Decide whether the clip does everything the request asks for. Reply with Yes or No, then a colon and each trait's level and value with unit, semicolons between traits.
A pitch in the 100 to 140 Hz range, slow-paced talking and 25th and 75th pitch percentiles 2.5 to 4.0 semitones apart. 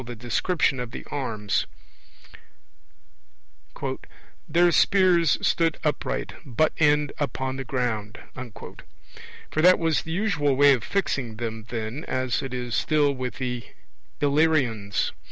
No: low, 135 Hz; slow, 120 wpm; average, 4.5 semitones